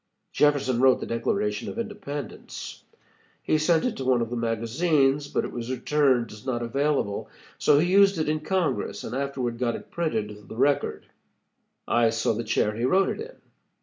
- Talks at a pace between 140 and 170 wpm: No, average, 185 wpm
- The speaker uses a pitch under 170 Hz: Yes, low, 135 Hz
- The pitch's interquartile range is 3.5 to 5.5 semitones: Yes, average, 4.7 semitones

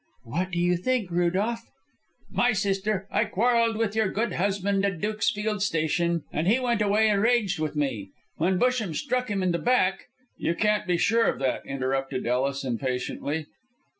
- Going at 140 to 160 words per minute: No, average, 175 wpm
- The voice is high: Yes, high, 195 Hz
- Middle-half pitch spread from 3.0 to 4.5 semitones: No, average, 5.2 semitones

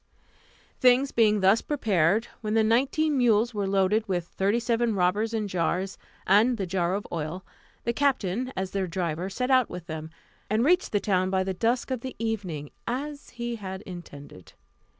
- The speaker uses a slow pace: No, average, 175 wpm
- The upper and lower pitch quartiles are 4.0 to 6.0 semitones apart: Yes, average, 4.3 semitones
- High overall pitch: Yes, high, 210 Hz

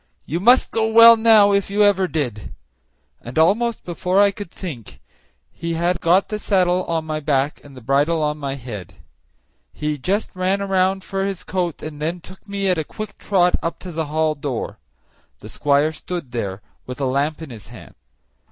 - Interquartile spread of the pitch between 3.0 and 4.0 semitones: No, average, 4.9 semitones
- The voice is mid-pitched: Yes, medium, 170 Hz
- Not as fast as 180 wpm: No, average, 190 wpm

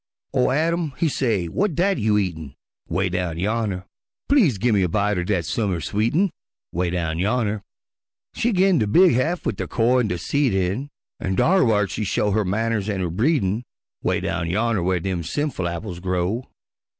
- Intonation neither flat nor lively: No, wide, 5.8 semitones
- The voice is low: Yes, low, 105 Hz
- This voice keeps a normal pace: Yes, average, 185 wpm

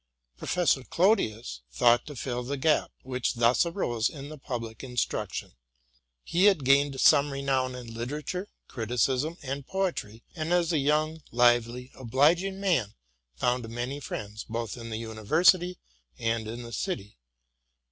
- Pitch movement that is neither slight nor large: Yes, average, 4.9 semitones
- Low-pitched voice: Yes, low, 130 Hz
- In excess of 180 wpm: No, average, 145 wpm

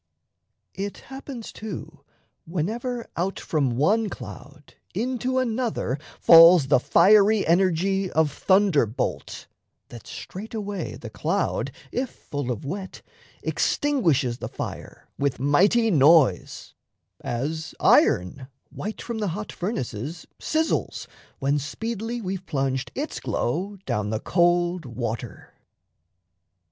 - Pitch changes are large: Yes, wide, 7.5 semitones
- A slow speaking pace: Yes, slow, 110 wpm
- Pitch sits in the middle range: Yes, medium, 175 Hz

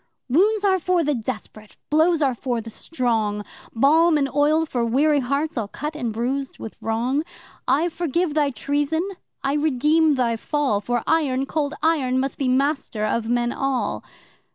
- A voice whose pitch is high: Yes, very high, 275 Hz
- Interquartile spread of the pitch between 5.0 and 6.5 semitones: No, average, 4.4 semitones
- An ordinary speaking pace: Yes, average, 165 wpm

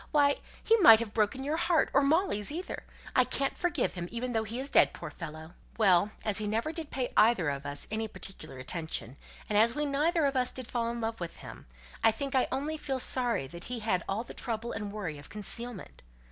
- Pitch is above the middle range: Yes, high, 230 Hz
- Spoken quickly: Yes, fast, 225 wpm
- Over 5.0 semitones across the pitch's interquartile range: Yes, wide, 5.4 semitones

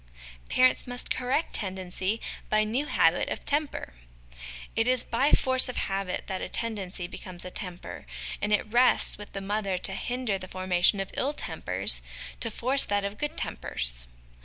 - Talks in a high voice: Yes, high, 210 Hz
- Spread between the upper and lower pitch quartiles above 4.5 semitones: Yes, average, 5.1 semitones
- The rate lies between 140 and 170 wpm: Yes, average, 165 wpm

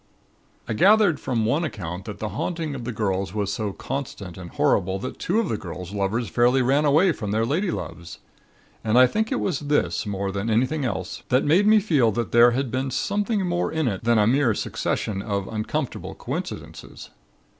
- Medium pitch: No, low, 120 Hz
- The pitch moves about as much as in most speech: No, wide, 6.7 semitones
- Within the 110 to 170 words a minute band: No, average, 195 wpm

